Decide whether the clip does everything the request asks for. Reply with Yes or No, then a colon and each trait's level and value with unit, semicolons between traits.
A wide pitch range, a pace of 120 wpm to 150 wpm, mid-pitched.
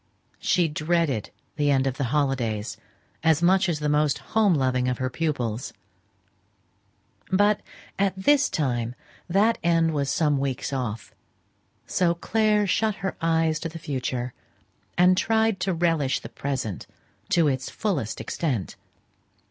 Yes: wide, 5.7 semitones; average, 140 wpm; medium, 155 Hz